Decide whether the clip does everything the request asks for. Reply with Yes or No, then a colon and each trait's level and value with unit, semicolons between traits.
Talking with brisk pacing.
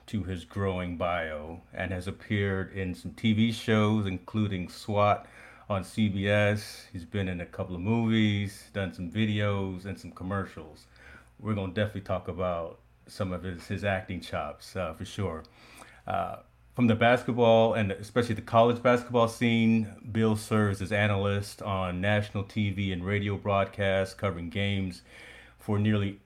No: average, 150 wpm